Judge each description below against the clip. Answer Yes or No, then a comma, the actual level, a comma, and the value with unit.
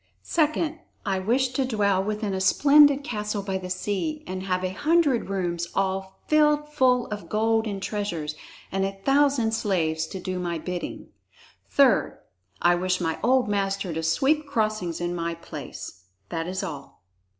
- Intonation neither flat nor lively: No, wide, 5.8 semitones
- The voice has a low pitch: No, high, 195 Hz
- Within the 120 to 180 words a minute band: Yes, average, 160 wpm